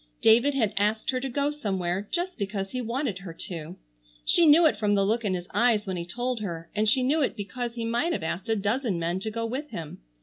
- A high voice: Yes, high, 220 Hz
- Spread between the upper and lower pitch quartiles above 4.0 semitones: Yes, average, 4.7 semitones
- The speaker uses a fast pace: Yes, fast, 245 wpm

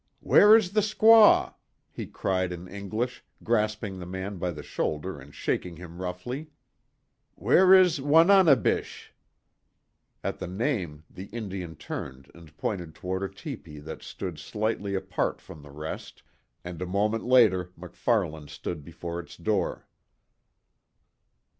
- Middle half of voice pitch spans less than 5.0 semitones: No, wide, 5.6 semitones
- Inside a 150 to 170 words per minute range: No, slow, 135 wpm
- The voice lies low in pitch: Yes, very low, 95 Hz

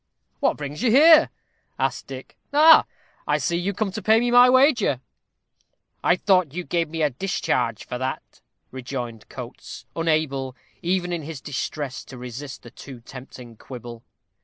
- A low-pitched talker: No, medium, 155 Hz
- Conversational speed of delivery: Yes, average, 160 wpm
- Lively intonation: Yes, wide, 7.2 semitones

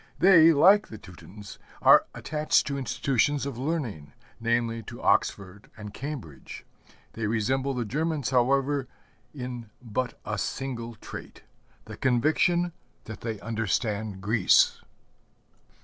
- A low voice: Yes, low, 120 Hz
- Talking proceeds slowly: Yes, slow, 115 wpm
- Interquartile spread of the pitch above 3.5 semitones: Yes, average, 4.6 semitones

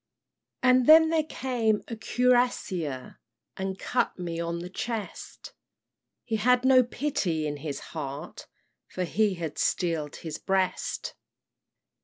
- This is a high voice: Yes, high, 195 Hz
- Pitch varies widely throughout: Yes, wide, 6.9 semitones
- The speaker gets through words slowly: Yes, slow, 125 wpm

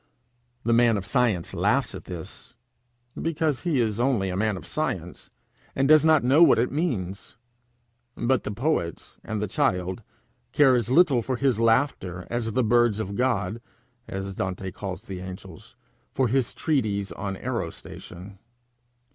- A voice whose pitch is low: Yes, low, 115 Hz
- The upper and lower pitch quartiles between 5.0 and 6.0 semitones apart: Yes, average, 5.3 semitones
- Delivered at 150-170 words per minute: Yes, average, 155 wpm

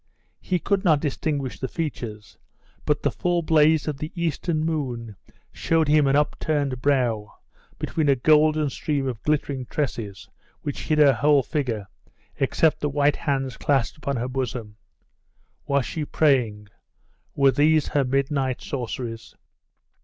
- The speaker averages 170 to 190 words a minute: No, average, 140 wpm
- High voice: No, medium, 140 Hz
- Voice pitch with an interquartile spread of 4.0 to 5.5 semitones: No, average, 3.2 semitones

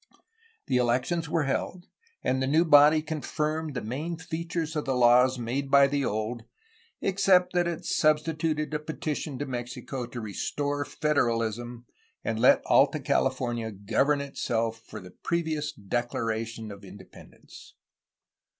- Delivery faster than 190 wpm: No, slow, 135 wpm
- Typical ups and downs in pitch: Yes, average, 4.6 semitones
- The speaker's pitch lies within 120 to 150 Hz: Yes, low, 135 Hz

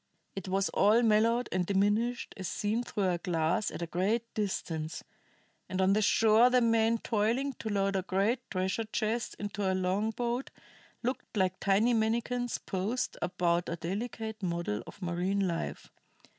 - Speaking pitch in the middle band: No, high, 205 Hz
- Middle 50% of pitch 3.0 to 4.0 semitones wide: Yes, average, 3.5 semitones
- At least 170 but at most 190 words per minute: No, average, 155 wpm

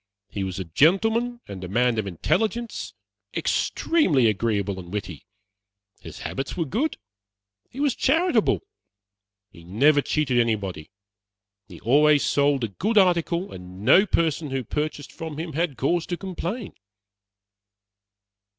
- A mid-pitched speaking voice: Yes, medium, 145 Hz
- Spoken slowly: Yes, slow, 130 wpm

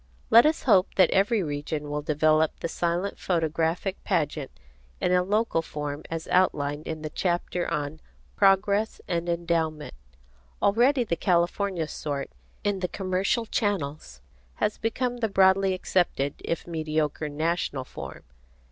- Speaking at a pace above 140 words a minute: No, slow, 135 wpm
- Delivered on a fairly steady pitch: No, average, 4.0 semitones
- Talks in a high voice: No, medium, 170 Hz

